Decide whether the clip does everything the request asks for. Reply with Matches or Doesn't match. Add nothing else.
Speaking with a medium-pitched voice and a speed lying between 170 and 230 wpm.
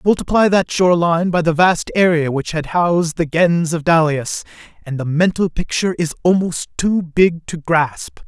Matches